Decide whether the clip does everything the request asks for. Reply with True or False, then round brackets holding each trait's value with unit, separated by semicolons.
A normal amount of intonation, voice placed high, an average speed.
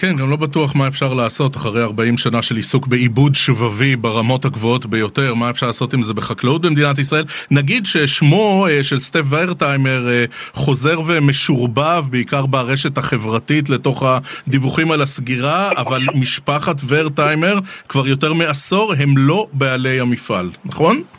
False (3.1 semitones; 135 Hz; 140 wpm)